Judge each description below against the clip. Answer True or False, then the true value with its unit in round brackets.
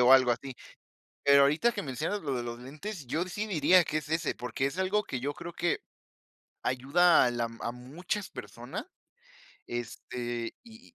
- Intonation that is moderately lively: False (6.2 semitones)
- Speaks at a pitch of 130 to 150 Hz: True (140 Hz)